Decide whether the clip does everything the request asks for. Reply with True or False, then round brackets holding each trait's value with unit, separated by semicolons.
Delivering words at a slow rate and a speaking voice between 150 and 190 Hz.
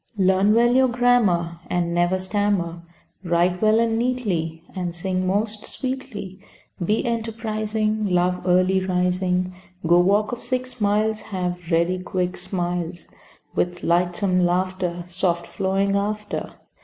True (125 wpm; 185 Hz)